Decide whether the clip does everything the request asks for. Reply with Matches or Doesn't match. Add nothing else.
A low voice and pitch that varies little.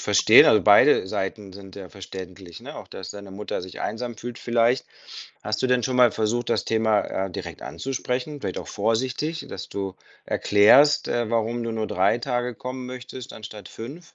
Doesn't match